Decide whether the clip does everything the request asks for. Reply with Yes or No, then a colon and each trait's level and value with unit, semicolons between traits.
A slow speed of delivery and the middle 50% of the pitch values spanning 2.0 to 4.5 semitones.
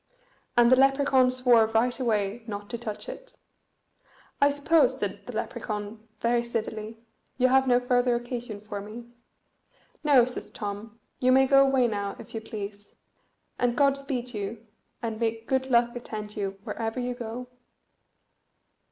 No: average, 150 wpm; average, 2.9 semitones